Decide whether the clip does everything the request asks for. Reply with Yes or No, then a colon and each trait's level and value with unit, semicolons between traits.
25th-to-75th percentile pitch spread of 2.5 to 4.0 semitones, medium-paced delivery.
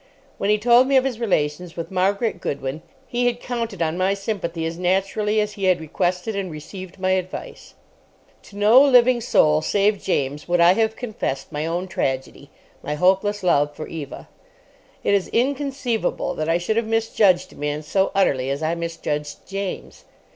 No: average, 5.1 semitones; average, 175 wpm